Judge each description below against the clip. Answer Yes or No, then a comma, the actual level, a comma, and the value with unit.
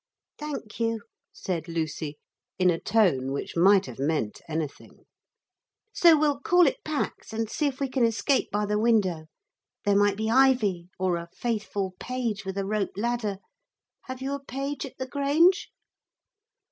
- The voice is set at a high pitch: Yes, high, 215 Hz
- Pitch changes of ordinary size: No, wide, 6.4 semitones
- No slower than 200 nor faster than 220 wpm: No, average, 160 wpm